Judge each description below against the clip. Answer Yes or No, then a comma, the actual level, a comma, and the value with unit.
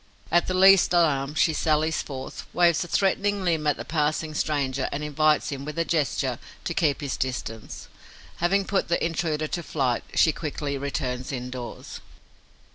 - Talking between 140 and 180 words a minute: Yes, average, 165 wpm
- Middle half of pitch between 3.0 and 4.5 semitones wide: Yes, average, 3.6 semitones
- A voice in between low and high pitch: Yes, medium, 155 Hz